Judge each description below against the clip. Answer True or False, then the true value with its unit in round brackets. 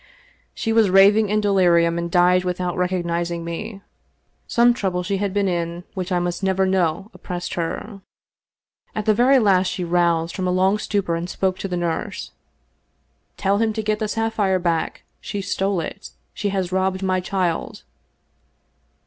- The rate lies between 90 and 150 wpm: False (170 wpm)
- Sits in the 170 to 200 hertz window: True (185 Hz)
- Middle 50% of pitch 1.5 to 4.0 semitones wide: True (2.5 semitones)